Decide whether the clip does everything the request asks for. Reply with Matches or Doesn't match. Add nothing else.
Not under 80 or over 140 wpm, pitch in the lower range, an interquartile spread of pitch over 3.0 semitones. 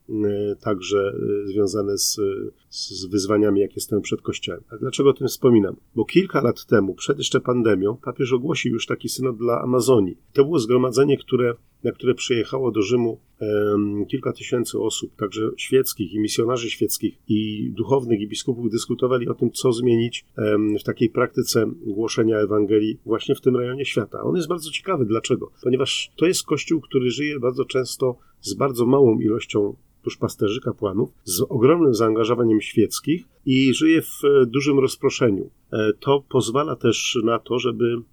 Doesn't match